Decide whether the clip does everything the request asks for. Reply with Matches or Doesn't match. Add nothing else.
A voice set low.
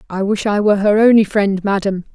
Doesn't match